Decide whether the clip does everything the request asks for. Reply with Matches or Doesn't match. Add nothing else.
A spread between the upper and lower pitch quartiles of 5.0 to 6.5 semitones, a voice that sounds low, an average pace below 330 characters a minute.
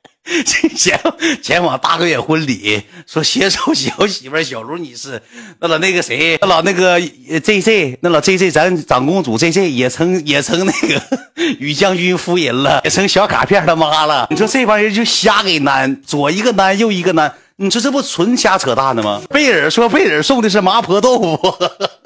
Doesn't match